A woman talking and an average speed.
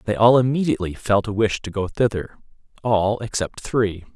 No: male; average, 175 wpm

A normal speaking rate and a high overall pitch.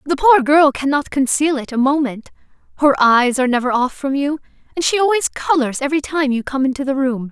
No: fast, 215 wpm; very high, 275 Hz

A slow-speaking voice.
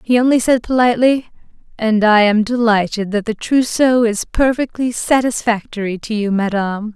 No: average, 145 wpm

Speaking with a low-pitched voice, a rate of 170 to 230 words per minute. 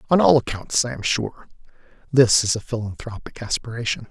No: low, 120 Hz; average, 160 wpm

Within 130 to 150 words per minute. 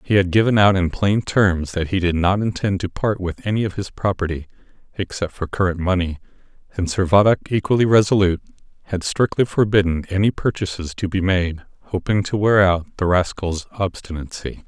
No: average, 170 wpm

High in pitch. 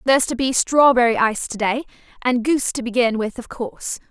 Yes: high, 245 Hz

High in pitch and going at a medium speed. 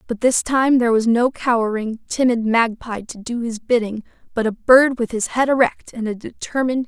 No: high, 235 Hz; fast, 210 wpm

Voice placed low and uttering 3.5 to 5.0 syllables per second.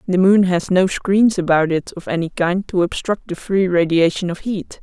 No: medium, 185 Hz; 4.7 syllables/s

